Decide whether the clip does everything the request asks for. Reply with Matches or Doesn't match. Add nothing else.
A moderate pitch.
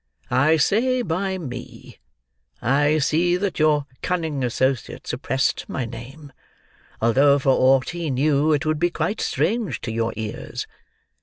Matches